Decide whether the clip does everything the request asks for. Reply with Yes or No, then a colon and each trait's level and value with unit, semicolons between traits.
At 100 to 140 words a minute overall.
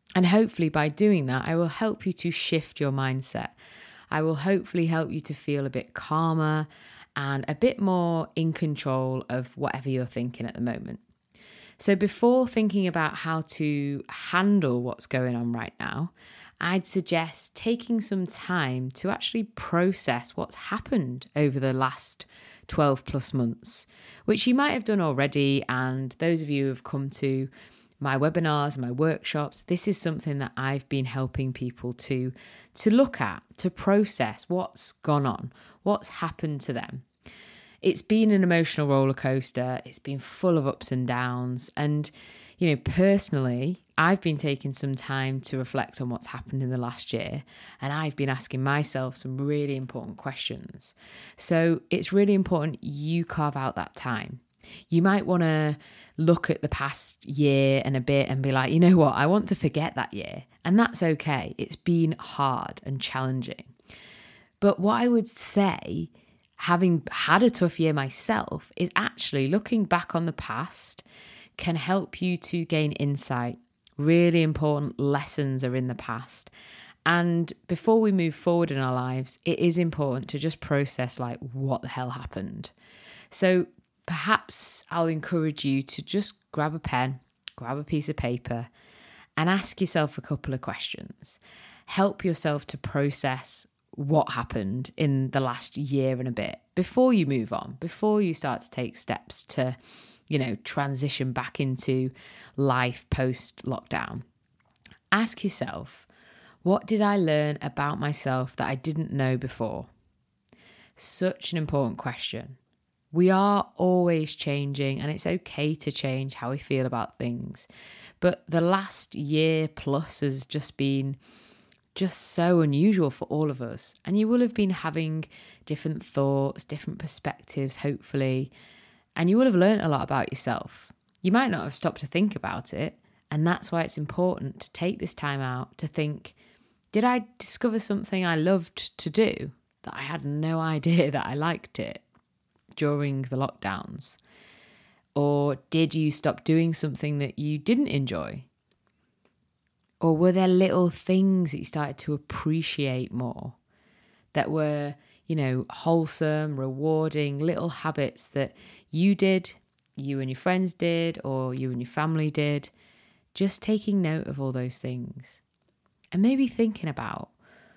No: average, 160 wpm